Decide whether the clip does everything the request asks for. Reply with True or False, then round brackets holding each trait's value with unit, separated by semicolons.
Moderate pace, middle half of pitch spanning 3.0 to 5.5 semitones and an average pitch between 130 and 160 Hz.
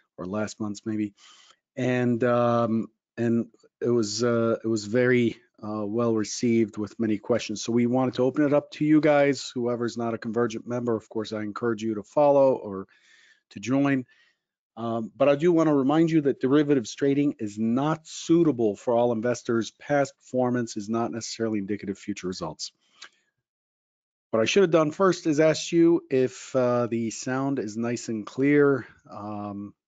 False (175 wpm; 4.0 semitones; 120 Hz)